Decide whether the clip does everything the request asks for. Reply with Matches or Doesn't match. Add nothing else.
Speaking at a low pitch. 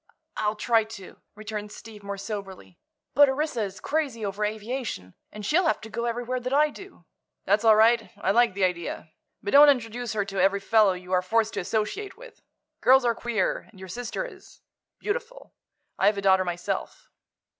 Doesn't match